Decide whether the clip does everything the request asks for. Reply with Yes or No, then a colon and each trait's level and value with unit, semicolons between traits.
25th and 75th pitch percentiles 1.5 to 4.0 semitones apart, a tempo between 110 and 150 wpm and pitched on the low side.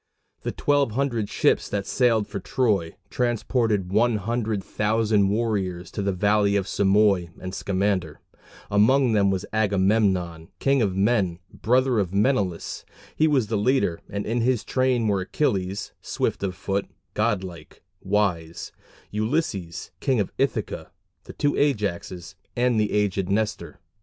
Yes: average, 3.5 semitones; average, 140 wpm; low, 105 Hz